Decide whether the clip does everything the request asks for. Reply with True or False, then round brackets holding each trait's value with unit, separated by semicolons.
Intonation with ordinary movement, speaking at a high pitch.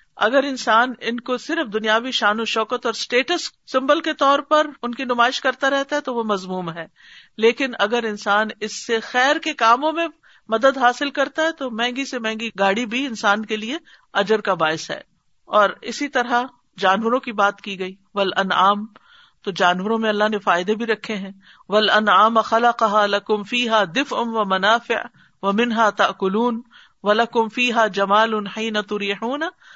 True (3.4 semitones; 225 Hz)